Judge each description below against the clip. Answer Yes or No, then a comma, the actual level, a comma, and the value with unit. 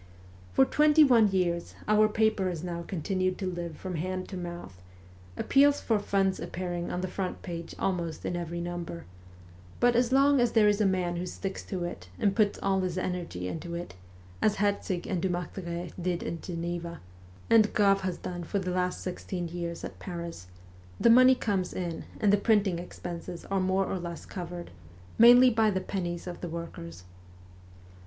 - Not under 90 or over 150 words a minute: No, average, 180 wpm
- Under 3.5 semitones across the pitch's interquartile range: Yes, average, 2.9 semitones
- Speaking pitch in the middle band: Yes, medium, 180 Hz